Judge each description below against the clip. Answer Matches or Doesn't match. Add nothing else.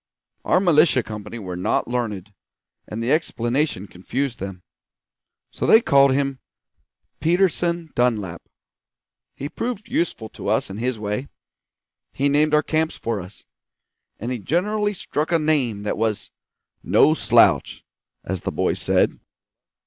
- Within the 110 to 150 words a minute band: Matches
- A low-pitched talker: Matches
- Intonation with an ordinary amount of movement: Doesn't match